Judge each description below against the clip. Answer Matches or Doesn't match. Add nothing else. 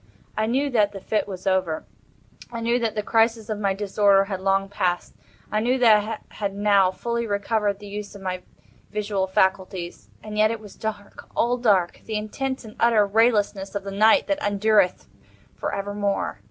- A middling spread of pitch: Doesn't match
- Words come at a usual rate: Matches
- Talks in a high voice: Matches